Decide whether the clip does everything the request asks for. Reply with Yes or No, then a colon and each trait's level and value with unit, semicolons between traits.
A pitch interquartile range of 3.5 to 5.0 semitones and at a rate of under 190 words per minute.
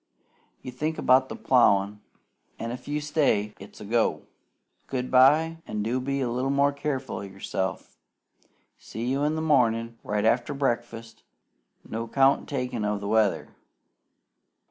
Yes: average, 3.8 semitones; average, 155 wpm